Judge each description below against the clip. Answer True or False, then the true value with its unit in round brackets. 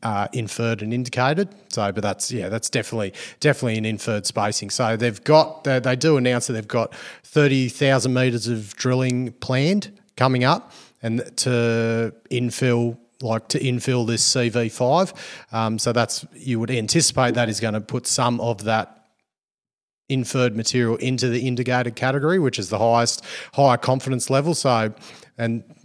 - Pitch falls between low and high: False (125 Hz)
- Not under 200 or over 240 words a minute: False (165 wpm)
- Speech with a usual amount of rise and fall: False (2.3 semitones)